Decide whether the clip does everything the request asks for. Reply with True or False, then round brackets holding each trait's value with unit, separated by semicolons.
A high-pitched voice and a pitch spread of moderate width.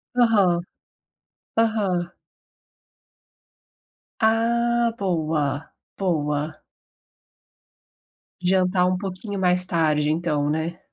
False (180 Hz; 4.3 semitones)